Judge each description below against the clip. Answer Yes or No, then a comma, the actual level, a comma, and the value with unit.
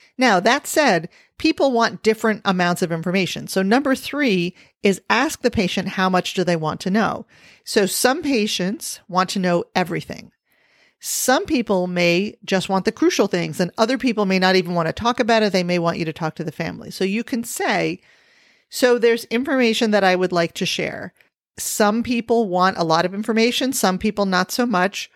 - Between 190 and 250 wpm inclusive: Yes, average, 200 wpm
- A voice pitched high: Yes, high, 200 Hz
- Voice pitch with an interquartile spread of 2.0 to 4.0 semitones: No, average, 4.5 semitones